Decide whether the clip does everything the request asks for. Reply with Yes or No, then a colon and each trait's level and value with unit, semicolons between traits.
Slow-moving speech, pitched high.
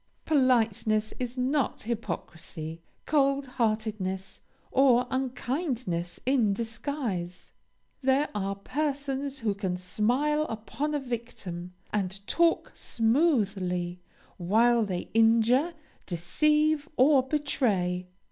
Yes: slow, 90 wpm; high, 235 Hz